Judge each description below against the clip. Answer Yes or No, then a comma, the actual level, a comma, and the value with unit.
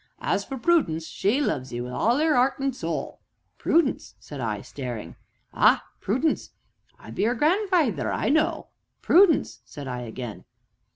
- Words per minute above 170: No, average, 160 wpm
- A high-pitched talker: Yes, high, 220 Hz